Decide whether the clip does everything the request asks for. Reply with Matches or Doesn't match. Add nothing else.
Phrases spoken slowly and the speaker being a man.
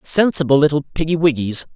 Matches